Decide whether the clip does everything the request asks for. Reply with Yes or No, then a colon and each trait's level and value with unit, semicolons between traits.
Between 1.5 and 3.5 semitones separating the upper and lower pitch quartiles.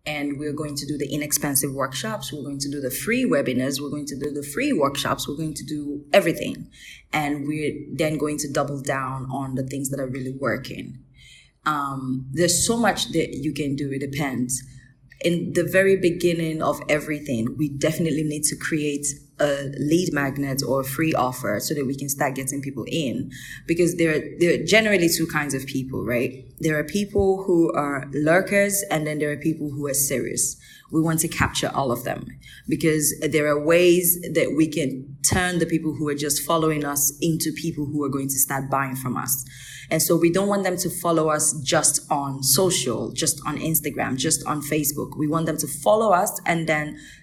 Yes: average, 2.7 semitones